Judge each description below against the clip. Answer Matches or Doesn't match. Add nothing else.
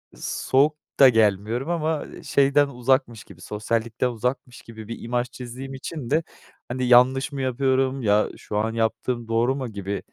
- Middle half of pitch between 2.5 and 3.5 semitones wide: Matches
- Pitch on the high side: Doesn't match